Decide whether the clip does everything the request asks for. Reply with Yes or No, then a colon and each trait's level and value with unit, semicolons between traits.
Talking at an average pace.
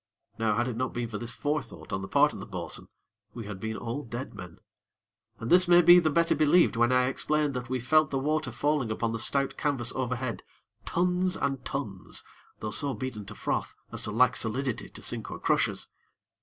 No: fast, 210 wpm